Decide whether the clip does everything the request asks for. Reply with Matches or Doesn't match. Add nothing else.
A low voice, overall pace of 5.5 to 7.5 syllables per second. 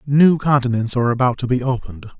Matches